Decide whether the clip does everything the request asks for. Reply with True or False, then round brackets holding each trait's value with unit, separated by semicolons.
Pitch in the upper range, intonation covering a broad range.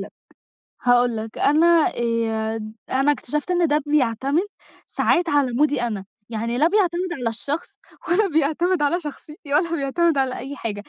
True (285 Hz; 5.7 semitones)